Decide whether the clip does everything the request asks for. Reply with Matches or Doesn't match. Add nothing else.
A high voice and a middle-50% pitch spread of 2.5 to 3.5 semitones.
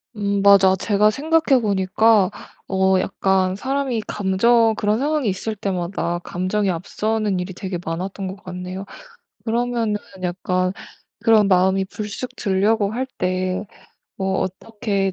Matches